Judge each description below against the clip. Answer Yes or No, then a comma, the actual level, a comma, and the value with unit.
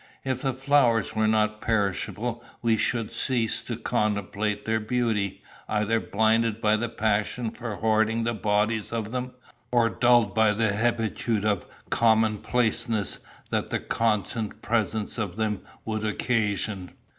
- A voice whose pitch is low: Yes, low, 110 Hz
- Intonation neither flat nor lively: No, narrow, 1.6 semitones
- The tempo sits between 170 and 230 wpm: No, slow, 135 wpm